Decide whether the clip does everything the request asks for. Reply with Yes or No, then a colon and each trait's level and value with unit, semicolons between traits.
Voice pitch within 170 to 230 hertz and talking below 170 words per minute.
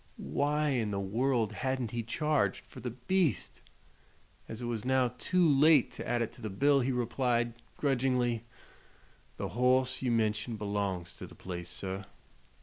No: low, 120 Hz; average, 160 wpm